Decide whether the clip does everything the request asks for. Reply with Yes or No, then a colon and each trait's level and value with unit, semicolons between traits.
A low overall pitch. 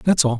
No: medium, 145 Hz